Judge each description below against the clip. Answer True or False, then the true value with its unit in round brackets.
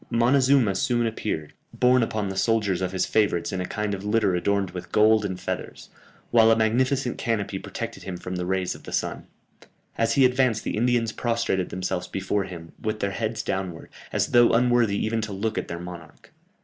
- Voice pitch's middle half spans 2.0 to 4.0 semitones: True (3.5 semitones)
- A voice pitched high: False (105 Hz)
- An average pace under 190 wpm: False (195 wpm)